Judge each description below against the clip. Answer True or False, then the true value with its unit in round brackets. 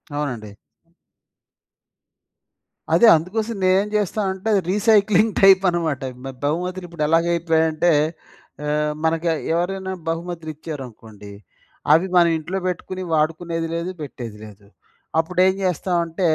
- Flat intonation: False (3.3 semitones)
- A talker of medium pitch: True (170 Hz)